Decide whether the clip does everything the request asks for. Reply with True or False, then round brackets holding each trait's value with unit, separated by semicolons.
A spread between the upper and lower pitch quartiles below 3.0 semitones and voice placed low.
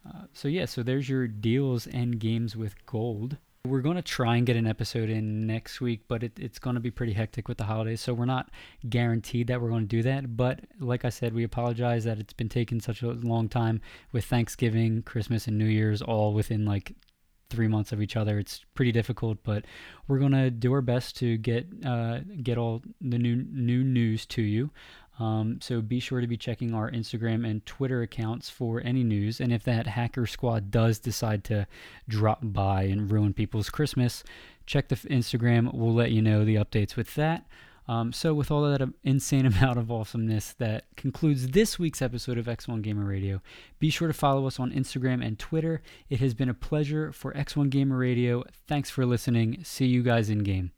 True (2.5 semitones; 120 Hz)